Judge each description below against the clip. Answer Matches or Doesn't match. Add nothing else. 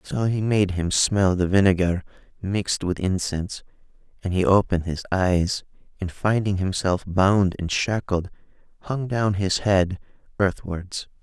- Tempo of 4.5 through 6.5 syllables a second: Doesn't match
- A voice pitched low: Matches